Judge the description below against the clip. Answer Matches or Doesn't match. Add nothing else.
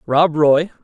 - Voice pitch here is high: Doesn't match